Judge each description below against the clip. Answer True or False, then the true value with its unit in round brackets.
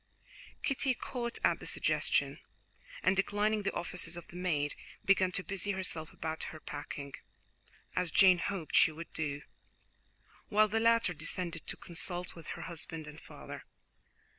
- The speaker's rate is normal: True (150 wpm)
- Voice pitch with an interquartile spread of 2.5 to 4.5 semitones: True (3.9 semitones)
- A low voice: False (180 Hz)